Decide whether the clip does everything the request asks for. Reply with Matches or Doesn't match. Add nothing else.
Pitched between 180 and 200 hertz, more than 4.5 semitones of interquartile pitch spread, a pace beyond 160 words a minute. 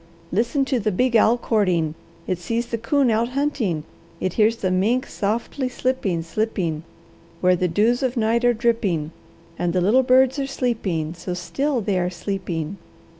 Doesn't match